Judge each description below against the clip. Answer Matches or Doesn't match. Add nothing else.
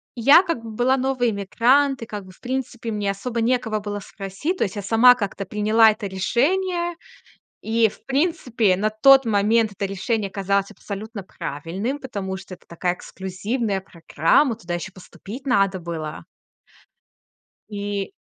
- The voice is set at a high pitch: Matches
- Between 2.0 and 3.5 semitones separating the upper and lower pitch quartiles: Doesn't match